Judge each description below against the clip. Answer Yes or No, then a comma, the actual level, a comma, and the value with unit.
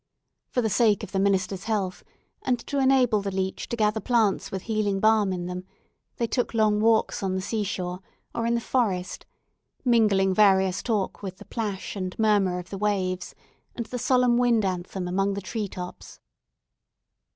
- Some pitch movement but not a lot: Yes, average, 3.1 semitones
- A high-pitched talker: Yes, high, 205 Hz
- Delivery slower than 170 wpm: No, average, 180 wpm